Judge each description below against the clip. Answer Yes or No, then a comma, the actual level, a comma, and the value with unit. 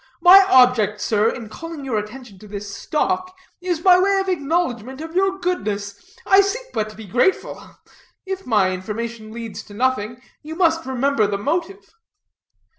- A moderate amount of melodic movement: No, wide, 8.8 semitones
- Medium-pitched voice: No, very high, 255 Hz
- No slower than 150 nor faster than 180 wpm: Yes, average, 165 wpm